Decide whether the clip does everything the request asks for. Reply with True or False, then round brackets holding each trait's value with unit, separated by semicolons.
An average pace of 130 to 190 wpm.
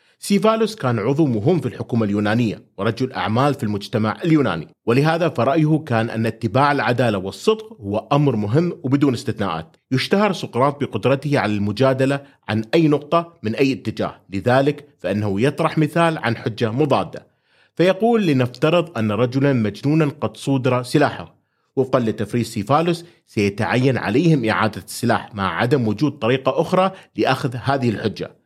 True (135 wpm)